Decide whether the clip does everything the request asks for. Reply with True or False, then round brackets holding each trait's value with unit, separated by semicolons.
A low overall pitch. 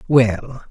True (120 Hz)